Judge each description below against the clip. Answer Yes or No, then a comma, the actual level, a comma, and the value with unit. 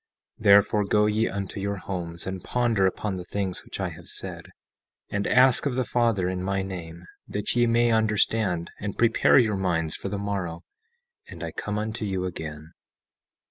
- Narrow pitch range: No, average, 3.1 semitones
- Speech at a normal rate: Yes, average, 180 wpm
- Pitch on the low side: Yes, low, 100 Hz